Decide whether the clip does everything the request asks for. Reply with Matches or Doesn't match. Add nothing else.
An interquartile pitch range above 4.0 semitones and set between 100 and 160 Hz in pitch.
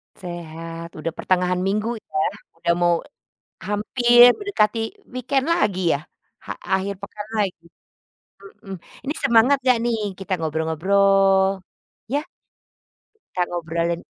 Doesn't match